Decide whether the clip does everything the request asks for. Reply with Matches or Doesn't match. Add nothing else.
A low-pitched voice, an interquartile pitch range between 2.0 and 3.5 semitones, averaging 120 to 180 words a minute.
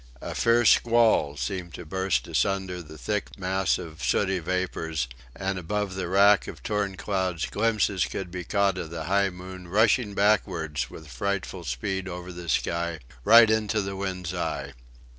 Matches